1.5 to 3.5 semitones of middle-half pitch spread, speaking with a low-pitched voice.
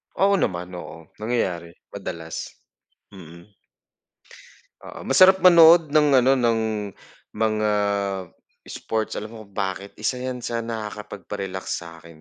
No: wide, 5.4 semitones; low, 105 Hz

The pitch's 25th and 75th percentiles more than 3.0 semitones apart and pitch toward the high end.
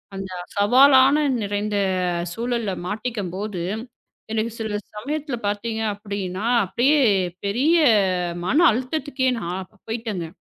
Yes: average, 4.0 semitones; high, 220 Hz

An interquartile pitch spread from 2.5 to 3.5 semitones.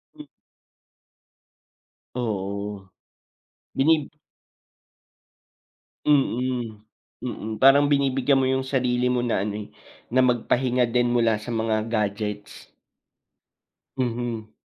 Yes: average, 3.0 semitones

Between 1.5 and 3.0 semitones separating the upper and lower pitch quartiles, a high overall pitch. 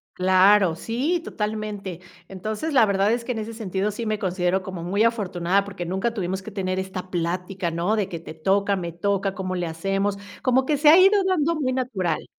No: average, 3.4 semitones; high, 195 Hz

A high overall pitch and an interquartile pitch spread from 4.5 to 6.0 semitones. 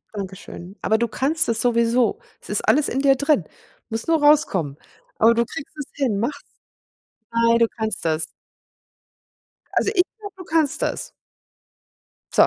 Yes: high, 235 Hz; average, 5.2 semitones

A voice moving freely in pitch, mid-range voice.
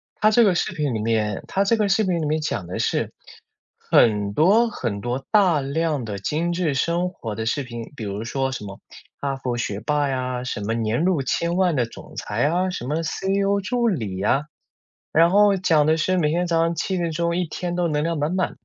Yes: wide, 6.8 semitones; medium, 155 Hz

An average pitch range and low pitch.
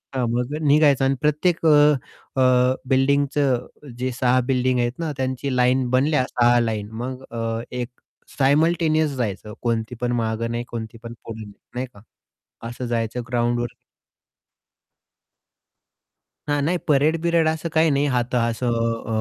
Yes: average, 3.4 semitones; low, 125 Hz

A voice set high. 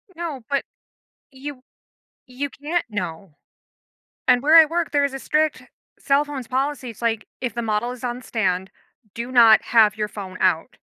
Yes: very high, 250 Hz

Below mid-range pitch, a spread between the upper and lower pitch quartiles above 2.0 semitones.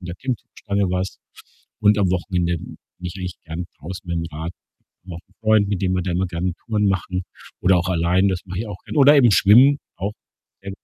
Yes: very low, 95 Hz; narrow, 2.5 semitones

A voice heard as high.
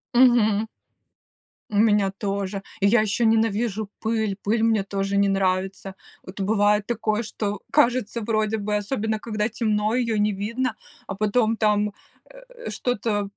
Yes: high, 215 Hz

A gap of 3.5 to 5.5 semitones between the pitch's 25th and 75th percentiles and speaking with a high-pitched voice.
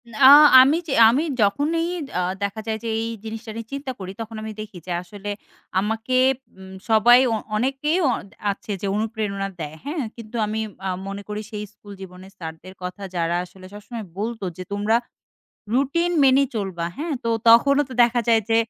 Yes: average, 3.8 semitones; high, 220 Hz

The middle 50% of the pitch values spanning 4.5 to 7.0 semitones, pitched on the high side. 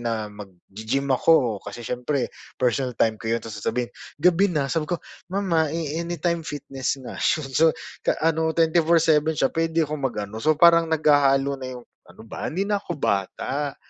No: average, 5.0 semitones; medium, 145 Hz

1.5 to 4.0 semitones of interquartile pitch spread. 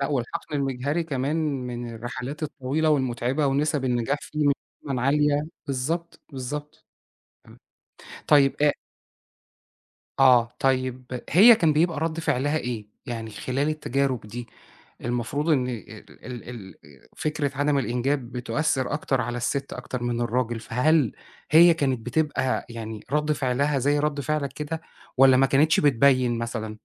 Yes: average, 3.4 semitones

